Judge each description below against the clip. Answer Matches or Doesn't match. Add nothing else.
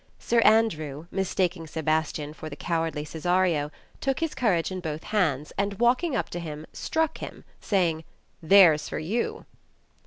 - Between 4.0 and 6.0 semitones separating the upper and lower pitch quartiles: Matches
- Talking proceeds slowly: Doesn't match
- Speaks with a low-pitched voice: Doesn't match